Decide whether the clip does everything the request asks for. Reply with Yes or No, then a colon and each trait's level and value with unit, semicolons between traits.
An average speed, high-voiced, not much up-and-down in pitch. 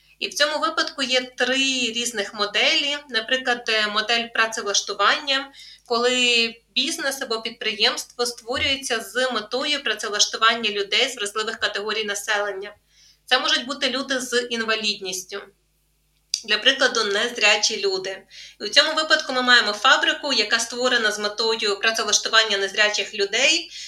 No: average, 120 wpm; high, 230 Hz; average, 3.8 semitones